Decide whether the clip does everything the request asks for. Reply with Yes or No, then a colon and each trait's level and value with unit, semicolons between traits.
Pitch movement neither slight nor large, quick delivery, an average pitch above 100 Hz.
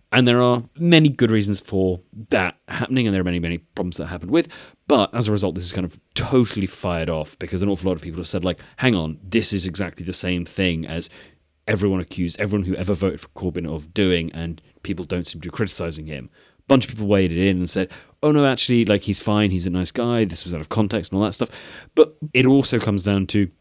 No: average, 4.0 semitones; fast, 250 wpm; very low, 95 Hz